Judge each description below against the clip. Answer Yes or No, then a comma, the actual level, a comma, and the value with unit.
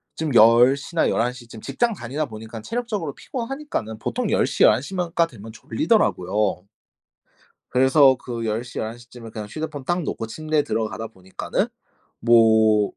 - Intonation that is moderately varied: No, wide, 5.9 semitones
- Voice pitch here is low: Yes, low, 120 Hz